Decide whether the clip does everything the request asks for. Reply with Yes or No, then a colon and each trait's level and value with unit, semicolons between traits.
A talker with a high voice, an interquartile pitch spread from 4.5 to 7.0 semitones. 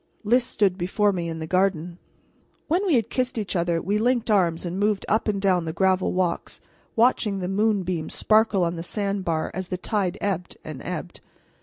No: high, 195 Hz; average, 3.3 semitones